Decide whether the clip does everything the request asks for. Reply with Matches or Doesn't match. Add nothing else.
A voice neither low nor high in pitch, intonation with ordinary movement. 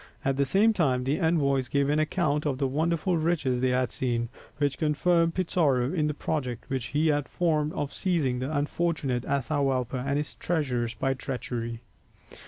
Matches